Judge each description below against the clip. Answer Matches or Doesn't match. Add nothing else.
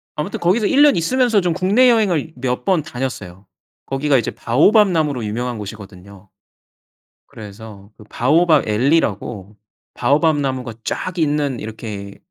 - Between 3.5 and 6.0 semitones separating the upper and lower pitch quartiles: Doesn't match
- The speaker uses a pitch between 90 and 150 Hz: Matches